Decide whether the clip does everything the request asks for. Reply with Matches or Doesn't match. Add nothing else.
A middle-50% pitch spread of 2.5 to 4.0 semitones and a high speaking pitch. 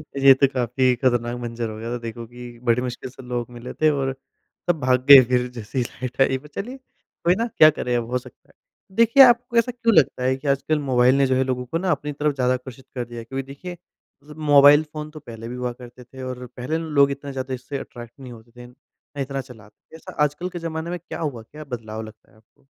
Doesn't match